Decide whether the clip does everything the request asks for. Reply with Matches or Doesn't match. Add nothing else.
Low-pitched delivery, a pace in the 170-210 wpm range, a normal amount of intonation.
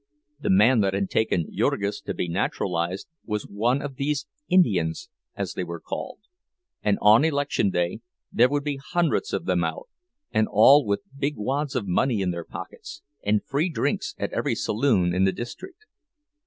Doesn't match